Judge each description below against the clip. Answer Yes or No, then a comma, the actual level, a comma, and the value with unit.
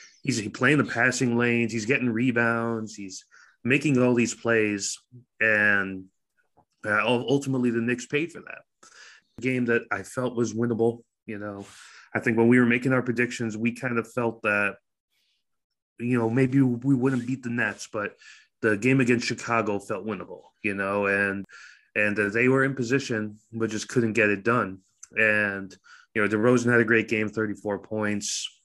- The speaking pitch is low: Yes, low, 115 Hz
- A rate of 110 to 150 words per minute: No, average, 170 wpm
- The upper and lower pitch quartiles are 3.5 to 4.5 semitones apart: No, average, 2.7 semitones